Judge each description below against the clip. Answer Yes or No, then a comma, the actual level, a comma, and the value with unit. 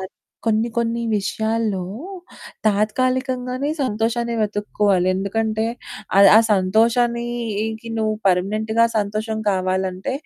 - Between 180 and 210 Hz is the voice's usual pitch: No, high, 220 Hz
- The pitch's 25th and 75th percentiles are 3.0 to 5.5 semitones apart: No, narrow, 2.6 semitones